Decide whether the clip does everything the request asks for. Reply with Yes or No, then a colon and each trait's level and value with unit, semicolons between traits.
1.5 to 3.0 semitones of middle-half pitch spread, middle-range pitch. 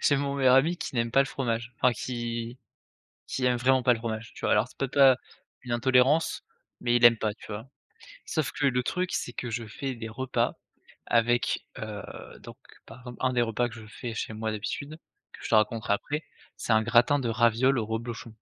No: narrow, 2.6 semitones; low, 120 Hz